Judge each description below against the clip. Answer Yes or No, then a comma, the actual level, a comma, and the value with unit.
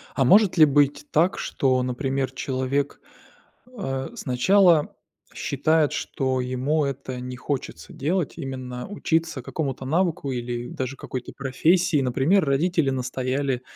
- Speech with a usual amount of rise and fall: Yes, average, 3.4 semitones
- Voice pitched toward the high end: No, low, 135 Hz